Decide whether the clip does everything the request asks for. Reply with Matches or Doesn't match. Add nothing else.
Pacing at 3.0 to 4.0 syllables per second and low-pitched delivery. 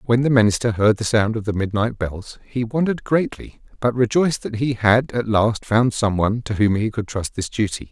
Doesn't match